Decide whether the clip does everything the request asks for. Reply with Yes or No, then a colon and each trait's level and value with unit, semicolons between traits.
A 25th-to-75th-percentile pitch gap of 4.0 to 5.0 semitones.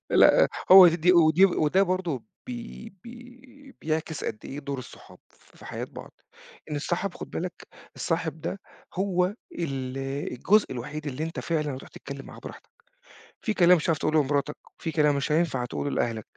Yes: average, 4.4 semitones